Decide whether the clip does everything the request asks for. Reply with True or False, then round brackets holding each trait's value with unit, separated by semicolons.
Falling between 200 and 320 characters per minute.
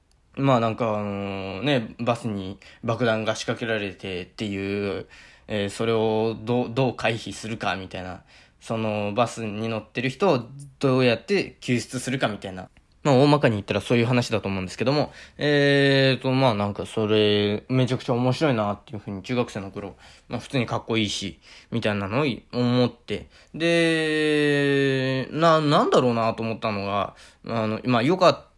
False (350 characters per minute)